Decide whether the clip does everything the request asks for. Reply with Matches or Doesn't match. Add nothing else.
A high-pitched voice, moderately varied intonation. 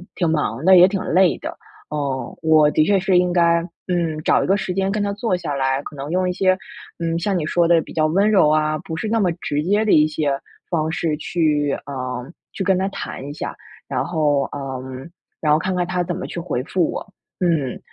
Doesn't match